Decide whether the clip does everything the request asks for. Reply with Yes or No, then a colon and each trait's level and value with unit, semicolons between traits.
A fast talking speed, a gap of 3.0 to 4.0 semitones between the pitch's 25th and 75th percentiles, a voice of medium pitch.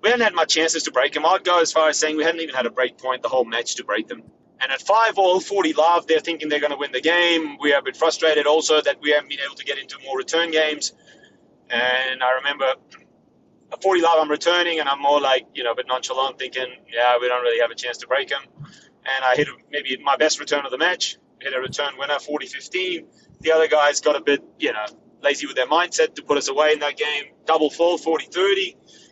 Yes: fast, 250 wpm; average, 3.3 semitones; medium, 150 Hz